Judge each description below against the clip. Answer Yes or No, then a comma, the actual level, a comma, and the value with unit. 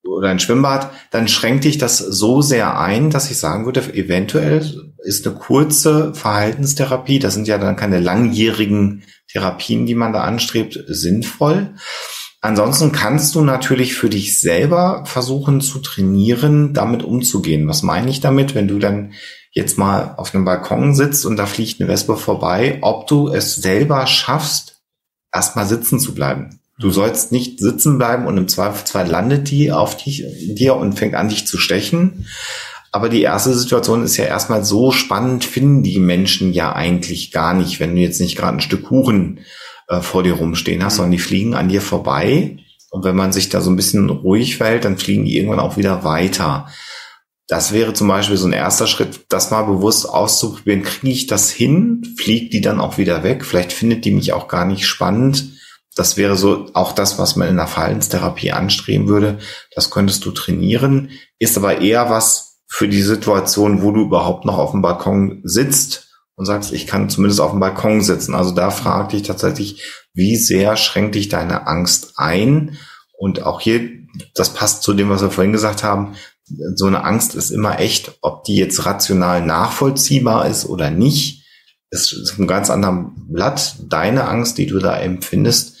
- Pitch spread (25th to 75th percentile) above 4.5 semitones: Yes, average, 5.3 semitones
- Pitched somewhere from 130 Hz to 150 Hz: No, low, 105 Hz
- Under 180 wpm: No, average, 185 wpm